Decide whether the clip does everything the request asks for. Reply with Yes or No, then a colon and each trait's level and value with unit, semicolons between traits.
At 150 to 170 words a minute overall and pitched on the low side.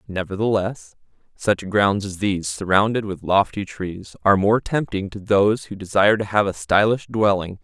Yes: average, 165 wpm; low, 100 Hz